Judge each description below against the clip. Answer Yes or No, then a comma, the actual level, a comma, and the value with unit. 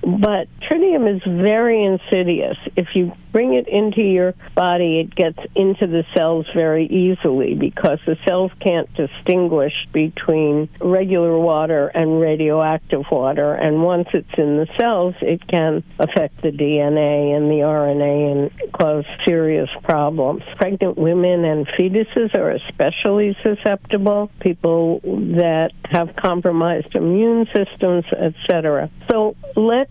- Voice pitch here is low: No, medium, 175 Hz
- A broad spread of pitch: No, average, 3.9 semitones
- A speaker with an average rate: No, slow, 130 wpm